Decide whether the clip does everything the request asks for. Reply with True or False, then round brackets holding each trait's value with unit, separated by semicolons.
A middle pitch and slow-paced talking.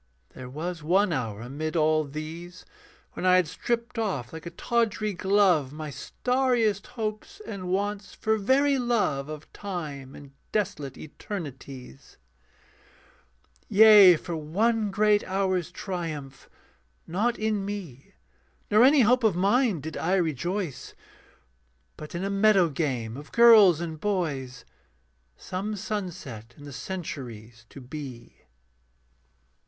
True (180 Hz; 125 wpm)